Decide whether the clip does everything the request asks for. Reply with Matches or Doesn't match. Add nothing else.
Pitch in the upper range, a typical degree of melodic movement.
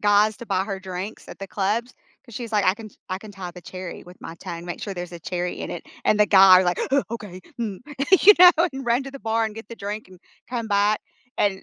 Matches